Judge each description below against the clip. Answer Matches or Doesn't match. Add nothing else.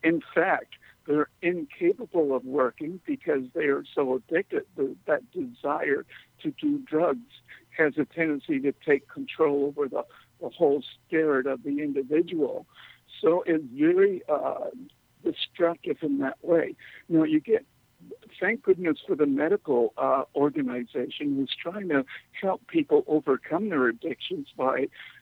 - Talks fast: Doesn't match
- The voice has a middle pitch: Matches